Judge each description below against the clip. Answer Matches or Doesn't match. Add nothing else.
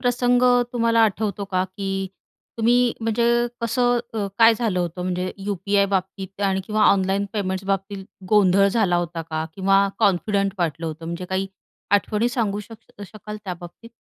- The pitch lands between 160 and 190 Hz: Doesn't match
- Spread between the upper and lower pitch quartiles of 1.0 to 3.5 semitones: Matches